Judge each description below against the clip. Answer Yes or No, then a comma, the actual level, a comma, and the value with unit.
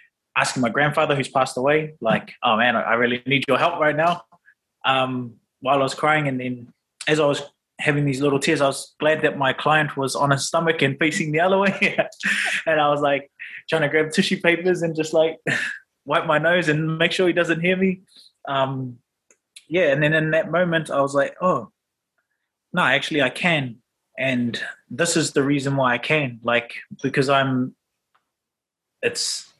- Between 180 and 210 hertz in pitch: No, medium, 145 Hz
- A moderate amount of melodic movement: Yes, average, 3.6 semitones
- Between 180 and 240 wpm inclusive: Yes, average, 190 wpm